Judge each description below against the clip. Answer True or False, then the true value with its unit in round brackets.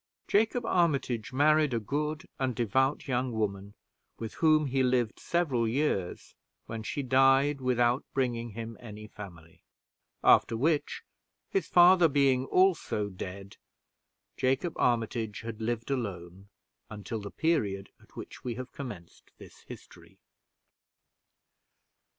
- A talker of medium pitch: False (125 Hz)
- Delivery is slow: True (120 wpm)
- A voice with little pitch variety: False (4.8 semitones)